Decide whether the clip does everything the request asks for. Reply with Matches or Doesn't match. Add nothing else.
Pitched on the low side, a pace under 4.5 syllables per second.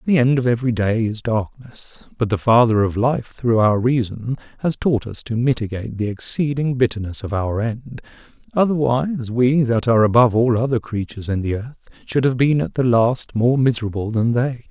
Doesn't match